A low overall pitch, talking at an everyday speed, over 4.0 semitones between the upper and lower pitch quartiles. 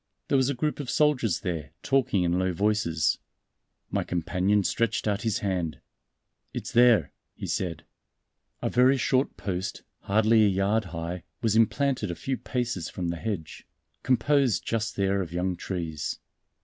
Yes: low, 100 Hz; average, 155 wpm; wide, 5.4 semitones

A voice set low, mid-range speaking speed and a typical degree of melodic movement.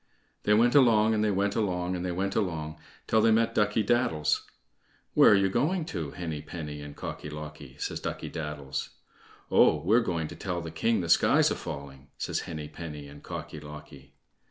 No: very low, 85 Hz; average, 190 wpm; wide, 5.9 semitones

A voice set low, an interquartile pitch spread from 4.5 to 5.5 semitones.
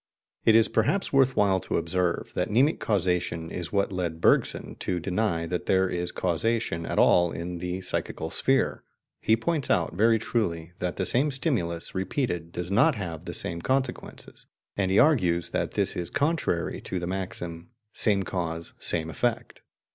Yes: very low, 95 Hz; average, 4.8 semitones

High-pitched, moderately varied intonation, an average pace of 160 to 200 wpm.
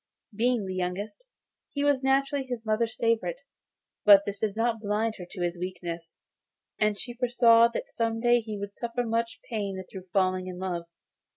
Yes: high, 220 Hz; average, 3.9 semitones; average, 175 wpm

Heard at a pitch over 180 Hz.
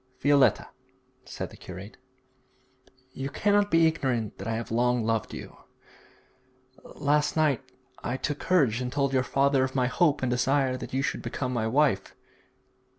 No: low, 130 Hz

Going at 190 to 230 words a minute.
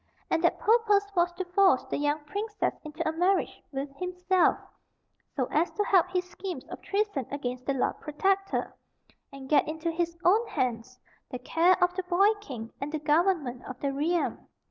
No: average, 180 wpm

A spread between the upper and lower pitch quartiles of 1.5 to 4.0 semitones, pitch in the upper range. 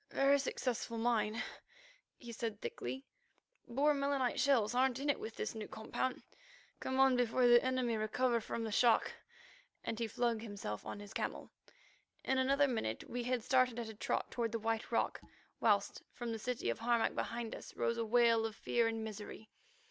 Yes: narrow, 2.5 semitones; high, 235 Hz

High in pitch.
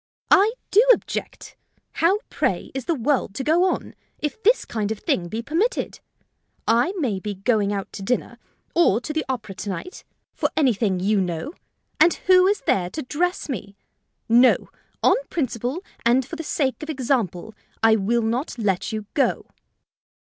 Yes: high, 245 Hz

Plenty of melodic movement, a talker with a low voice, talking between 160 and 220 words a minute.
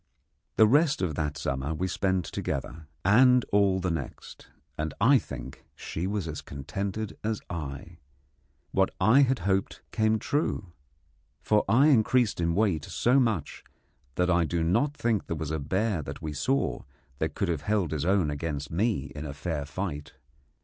Yes: wide, 5.8 semitones; very low, 95 Hz; average, 165 wpm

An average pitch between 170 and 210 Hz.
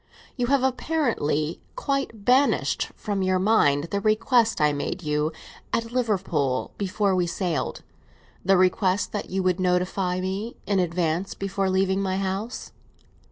Yes: high, 190 Hz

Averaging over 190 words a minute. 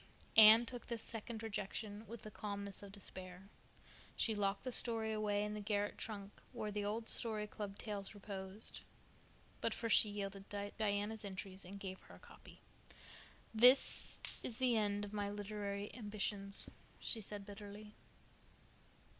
No: average, 155 wpm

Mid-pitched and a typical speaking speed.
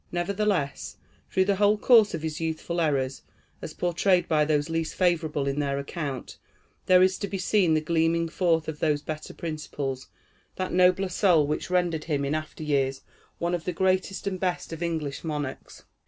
Yes: medium, 165 Hz; average, 180 wpm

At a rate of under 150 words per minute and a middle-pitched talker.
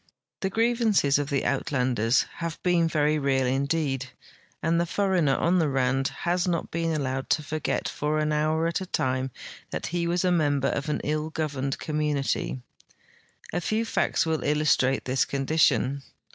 No: average, 170 wpm; medium, 150 Hz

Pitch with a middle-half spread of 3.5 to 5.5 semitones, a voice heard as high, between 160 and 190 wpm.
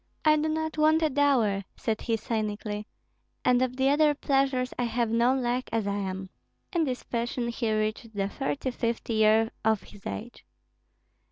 Yes: average, 3.8 semitones; high, 235 Hz; average, 175 wpm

